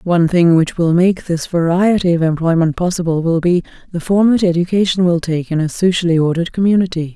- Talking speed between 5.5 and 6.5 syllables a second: Yes, 5.9 syllables/s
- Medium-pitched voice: Yes, medium, 175 Hz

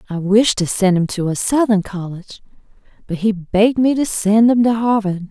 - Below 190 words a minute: No, fast, 205 wpm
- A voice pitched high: Yes, high, 210 Hz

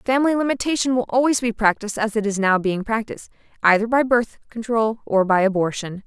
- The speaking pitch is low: No, high, 225 Hz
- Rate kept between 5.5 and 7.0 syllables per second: Yes, 6.0 syllables/s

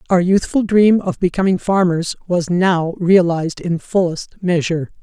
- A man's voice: No, female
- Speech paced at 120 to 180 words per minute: Yes, average, 145 wpm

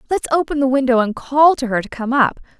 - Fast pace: Yes, fast, 255 wpm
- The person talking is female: Yes, female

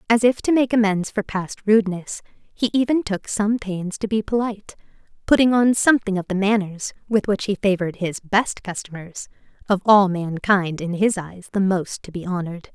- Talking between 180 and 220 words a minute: Yes, average, 190 wpm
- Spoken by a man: No, female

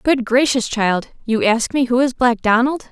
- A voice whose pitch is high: Yes, high, 240 Hz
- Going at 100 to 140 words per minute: No, fast, 205 wpm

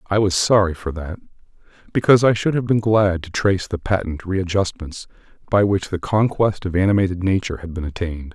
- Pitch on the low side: Yes, very low, 95 Hz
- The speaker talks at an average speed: Yes, average, 185 wpm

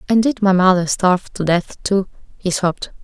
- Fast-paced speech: No, average, 195 wpm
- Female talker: Yes, female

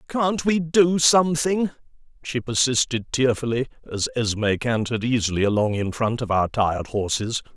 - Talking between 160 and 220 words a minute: No, average, 145 wpm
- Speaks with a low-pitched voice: Yes, low, 125 Hz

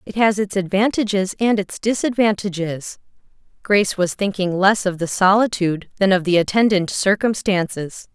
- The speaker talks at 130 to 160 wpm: Yes, average, 140 wpm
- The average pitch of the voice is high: Yes, high, 195 Hz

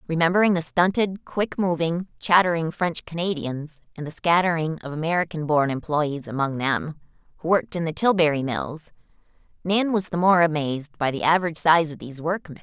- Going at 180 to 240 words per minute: No, average, 165 wpm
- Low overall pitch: No, medium, 165 Hz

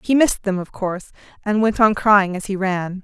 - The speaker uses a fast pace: Yes, fast, 235 wpm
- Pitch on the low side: No, high, 200 Hz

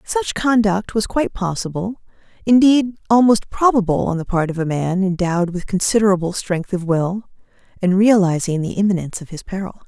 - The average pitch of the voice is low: No, high, 195 Hz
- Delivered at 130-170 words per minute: Yes, average, 165 wpm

